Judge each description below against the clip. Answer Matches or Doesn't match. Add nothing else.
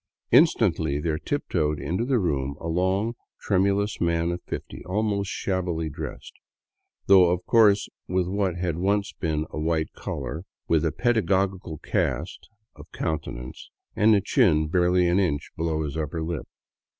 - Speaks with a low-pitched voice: Matches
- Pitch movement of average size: Matches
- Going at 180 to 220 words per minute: Doesn't match